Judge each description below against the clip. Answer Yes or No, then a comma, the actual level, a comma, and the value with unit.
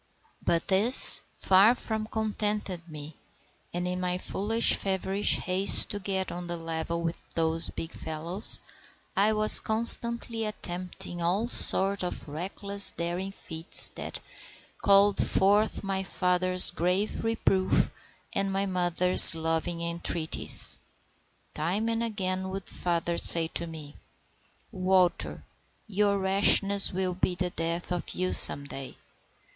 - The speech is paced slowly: Yes, slow, 125 wpm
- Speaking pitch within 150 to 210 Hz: Yes, medium, 185 Hz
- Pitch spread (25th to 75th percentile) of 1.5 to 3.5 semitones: Yes, average, 2.8 semitones